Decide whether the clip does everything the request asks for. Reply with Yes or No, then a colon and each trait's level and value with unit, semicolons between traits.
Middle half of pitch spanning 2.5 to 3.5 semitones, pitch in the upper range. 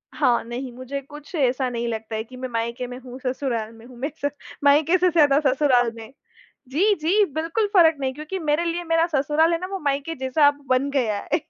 No: average, 4.2 semitones; very high, 275 Hz